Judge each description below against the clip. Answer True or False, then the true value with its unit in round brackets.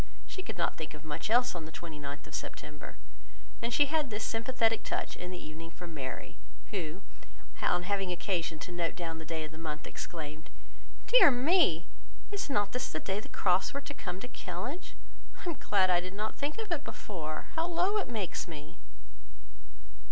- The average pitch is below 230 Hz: True (185 Hz)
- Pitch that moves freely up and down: True (7.5 semitones)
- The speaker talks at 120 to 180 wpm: False (195 wpm)